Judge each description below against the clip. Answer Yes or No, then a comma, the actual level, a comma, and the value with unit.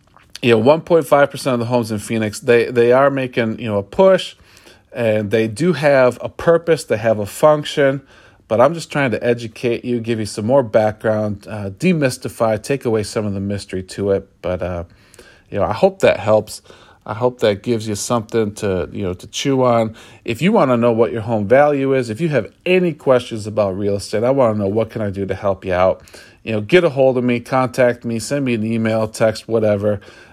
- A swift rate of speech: Yes, fast, 230 wpm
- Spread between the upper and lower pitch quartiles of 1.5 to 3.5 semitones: No, average, 3.9 semitones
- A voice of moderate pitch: No, low, 115 Hz